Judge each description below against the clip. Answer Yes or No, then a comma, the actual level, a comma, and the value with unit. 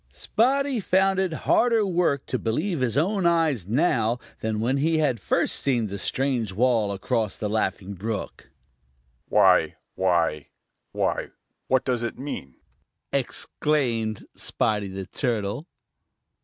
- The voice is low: Yes, low, 125 Hz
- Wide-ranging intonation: Yes, wide, 7.1 semitones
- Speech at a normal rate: No, slow, 130 wpm